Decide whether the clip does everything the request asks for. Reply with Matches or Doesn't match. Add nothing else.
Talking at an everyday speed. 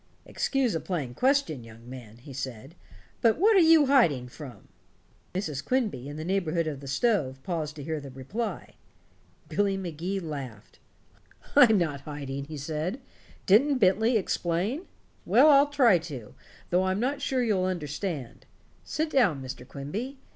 Matches